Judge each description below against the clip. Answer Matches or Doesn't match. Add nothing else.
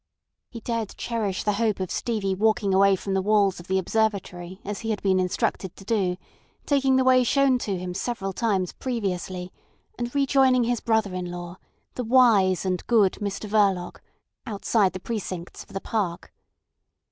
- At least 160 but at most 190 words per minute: Matches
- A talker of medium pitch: Doesn't match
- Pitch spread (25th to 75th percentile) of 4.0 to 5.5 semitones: Doesn't match